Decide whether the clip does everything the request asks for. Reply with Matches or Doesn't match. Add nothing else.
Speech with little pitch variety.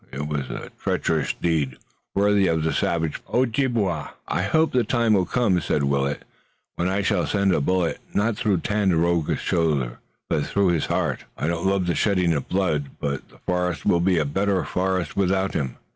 Doesn't match